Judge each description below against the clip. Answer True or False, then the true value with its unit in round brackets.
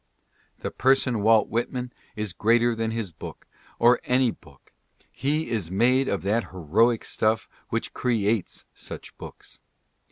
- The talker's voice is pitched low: True (115 Hz)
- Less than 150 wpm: True (135 wpm)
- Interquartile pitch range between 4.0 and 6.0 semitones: False (3.0 semitones)